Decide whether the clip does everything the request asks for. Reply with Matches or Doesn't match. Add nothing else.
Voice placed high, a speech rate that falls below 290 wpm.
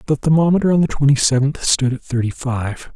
Doesn't match